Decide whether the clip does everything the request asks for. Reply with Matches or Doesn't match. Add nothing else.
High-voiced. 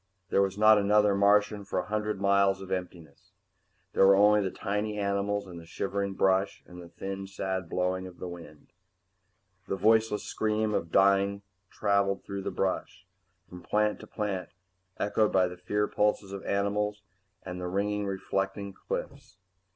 Doesn't match